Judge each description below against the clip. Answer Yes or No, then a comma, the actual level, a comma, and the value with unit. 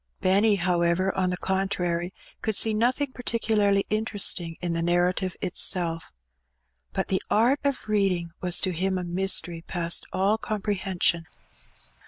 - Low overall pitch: No, high, 190 Hz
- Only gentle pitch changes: No, average, 3.1 semitones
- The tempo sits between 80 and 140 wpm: Yes, slow, 135 wpm